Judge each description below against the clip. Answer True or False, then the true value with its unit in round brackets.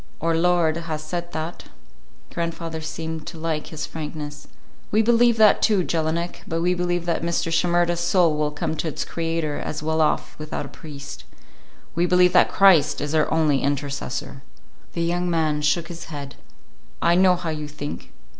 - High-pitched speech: False (165 Hz)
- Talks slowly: False (175 wpm)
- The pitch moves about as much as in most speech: False (2.2 semitones)